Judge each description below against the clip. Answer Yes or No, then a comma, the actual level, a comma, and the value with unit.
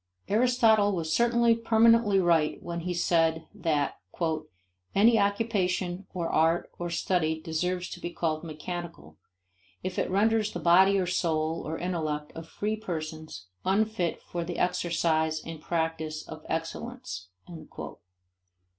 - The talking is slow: Yes, slow, 130 wpm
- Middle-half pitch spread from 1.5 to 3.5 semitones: No, average, 3.9 semitones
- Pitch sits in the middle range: Yes, medium, 175 Hz